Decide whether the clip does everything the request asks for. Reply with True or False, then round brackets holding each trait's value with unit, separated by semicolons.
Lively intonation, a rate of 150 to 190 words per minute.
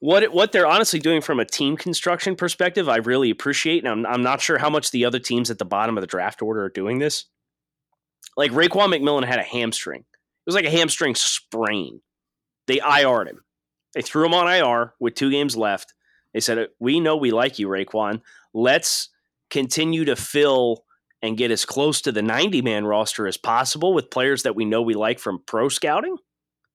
False (5.7 semitones; 205 wpm)